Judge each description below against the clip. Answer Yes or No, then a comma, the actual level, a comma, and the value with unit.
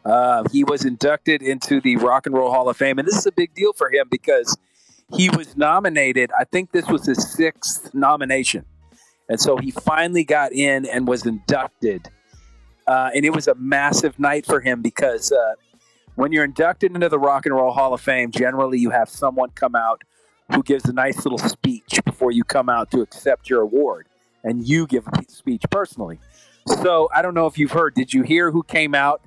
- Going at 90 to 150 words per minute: No, fast, 205 wpm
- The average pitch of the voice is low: No, medium, 150 Hz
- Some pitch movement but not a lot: No, wide, 6.8 semitones